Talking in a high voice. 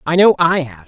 No: medium, 175 Hz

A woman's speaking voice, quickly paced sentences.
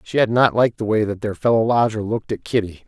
No: male; fast, 270 wpm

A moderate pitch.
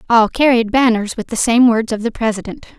No: high, 230 Hz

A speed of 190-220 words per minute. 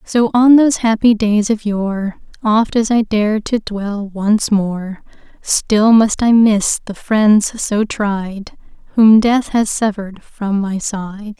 No: average, 160 wpm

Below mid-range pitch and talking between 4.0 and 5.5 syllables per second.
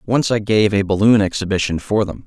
Yes: low, 105 Hz; 5.4 syllables/s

